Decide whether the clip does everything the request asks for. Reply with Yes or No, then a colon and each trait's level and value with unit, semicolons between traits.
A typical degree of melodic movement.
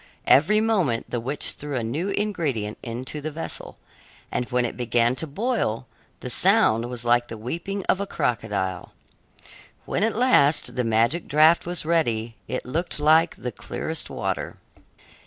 No: wide, 6.2 semitones